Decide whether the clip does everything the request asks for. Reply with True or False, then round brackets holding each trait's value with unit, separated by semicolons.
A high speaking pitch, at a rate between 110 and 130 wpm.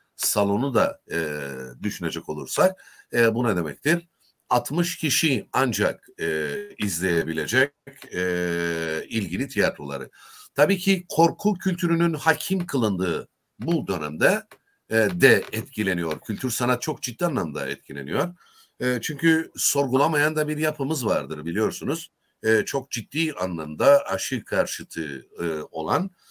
False (135 Hz; 115 wpm)